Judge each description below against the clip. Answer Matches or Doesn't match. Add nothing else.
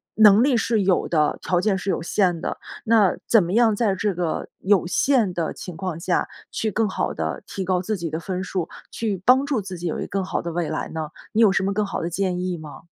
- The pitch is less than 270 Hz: Matches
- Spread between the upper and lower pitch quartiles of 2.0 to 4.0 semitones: Matches